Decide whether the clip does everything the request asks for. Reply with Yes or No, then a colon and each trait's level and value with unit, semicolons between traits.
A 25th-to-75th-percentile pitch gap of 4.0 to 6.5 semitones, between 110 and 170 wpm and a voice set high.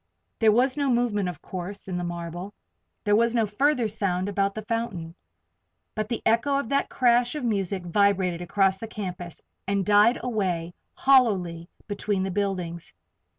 Yes: average, 4.3 semitones; average, 160 wpm; high, 205 Hz